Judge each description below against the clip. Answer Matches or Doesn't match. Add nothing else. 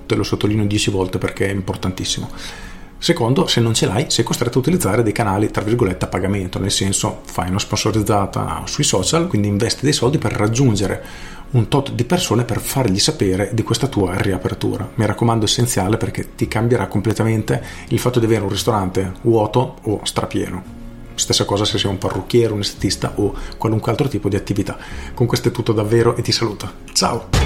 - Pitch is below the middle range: Matches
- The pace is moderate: Doesn't match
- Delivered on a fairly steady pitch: Doesn't match